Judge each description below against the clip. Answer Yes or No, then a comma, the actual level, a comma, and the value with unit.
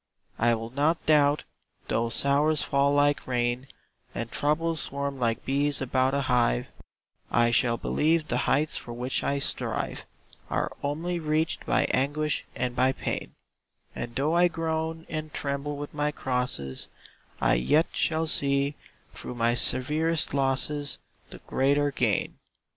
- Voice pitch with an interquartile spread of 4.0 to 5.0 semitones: No, average, 3.4 semitones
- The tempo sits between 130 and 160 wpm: Yes, average, 140 wpm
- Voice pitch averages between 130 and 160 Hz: Yes, medium, 140 Hz